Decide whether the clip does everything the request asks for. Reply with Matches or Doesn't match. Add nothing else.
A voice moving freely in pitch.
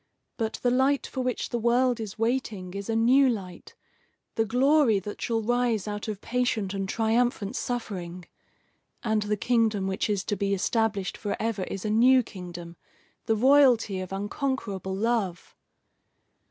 Doesn't match